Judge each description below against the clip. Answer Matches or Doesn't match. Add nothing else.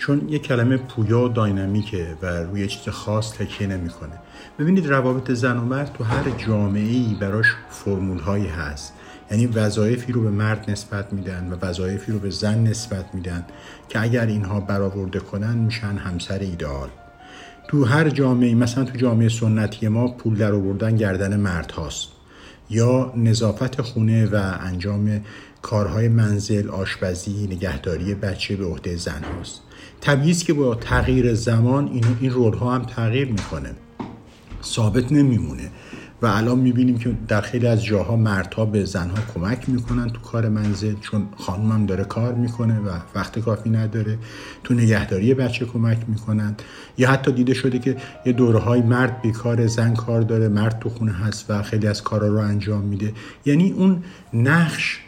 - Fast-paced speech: Matches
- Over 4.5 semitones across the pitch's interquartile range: Doesn't match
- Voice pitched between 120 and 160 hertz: Doesn't match